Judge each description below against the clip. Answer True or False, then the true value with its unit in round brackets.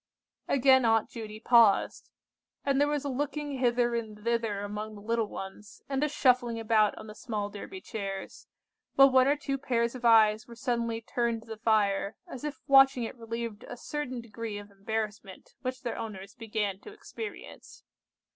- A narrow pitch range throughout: False (3.4 semitones)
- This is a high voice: True (230 Hz)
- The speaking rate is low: False (175 wpm)